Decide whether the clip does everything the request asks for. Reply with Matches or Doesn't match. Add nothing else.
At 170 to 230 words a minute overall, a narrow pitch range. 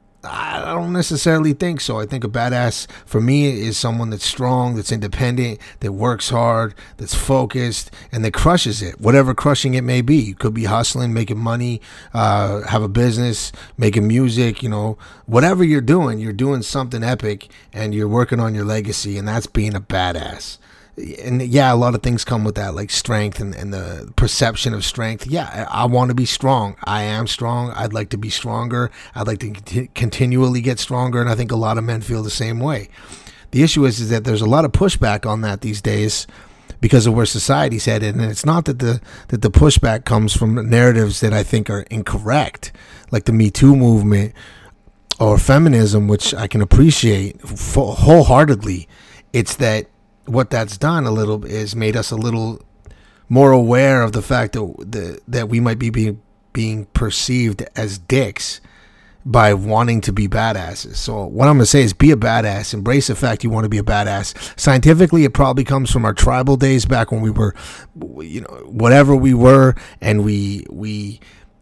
Doesn't match